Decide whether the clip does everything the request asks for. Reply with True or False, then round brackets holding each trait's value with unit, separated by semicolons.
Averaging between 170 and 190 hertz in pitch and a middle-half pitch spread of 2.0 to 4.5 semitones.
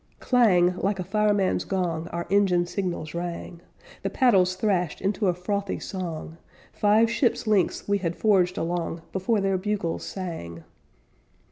True (185 Hz; 2.8 semitones)